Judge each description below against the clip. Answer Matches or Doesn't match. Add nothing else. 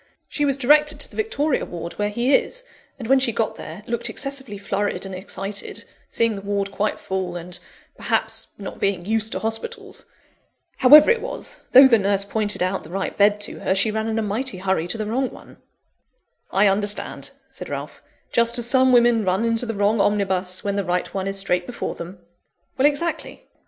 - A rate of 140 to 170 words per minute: Doesn't match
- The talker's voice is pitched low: Doesn't match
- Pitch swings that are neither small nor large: Matches